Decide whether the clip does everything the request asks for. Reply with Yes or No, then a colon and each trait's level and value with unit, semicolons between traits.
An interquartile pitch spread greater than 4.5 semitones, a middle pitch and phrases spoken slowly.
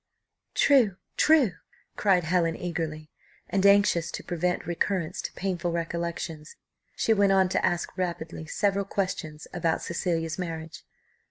No: average, 2.9 semitones; medium, 175 Hz; slow, 125 wpm